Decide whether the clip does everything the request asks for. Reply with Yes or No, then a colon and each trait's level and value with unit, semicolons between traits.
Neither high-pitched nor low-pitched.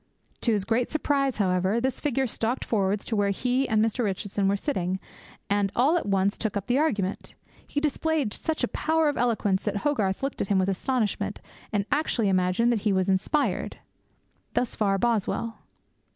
No: high, 220 Hz